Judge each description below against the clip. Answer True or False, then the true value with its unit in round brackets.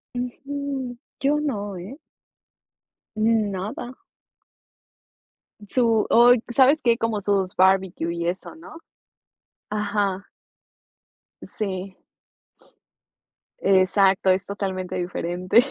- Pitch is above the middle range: True (205 Hz)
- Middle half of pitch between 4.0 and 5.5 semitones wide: True (4.4 semitones)